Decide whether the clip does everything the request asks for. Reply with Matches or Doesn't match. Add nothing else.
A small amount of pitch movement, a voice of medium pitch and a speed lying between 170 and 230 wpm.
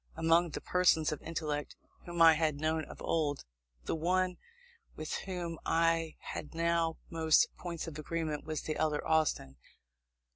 Doesn't match